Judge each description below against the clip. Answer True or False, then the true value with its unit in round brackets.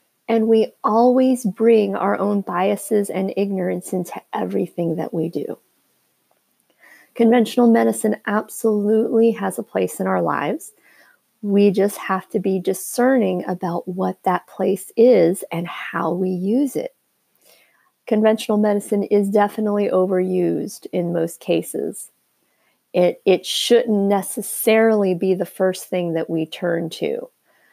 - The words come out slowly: True (130 wpm)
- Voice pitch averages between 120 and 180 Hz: False (200 Hz)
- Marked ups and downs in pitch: False (3.3 semitones)